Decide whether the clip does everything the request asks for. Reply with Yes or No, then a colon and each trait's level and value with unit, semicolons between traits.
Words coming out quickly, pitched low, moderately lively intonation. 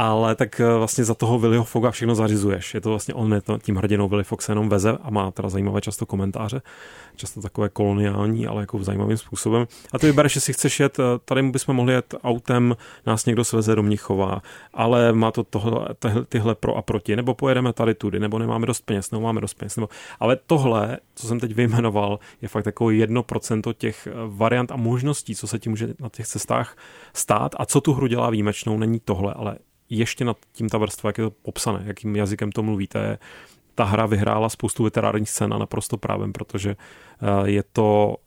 No: fast, 200 wpm; low, 110 Hz; narrow, 2.2 semitones